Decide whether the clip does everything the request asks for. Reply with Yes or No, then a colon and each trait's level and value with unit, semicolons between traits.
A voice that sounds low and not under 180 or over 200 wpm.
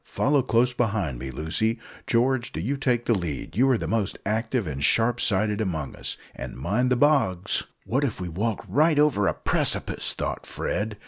Yes: low, 110 Hz; average, 190 wpm